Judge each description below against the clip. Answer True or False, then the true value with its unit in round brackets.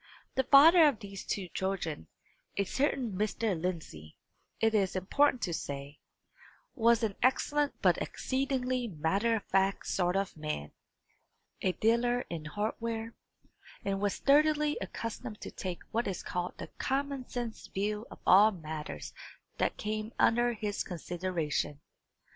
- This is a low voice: False (210 Hz)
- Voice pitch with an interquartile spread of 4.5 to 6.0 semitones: True (5.0 semitones)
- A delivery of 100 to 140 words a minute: True (135 wpm)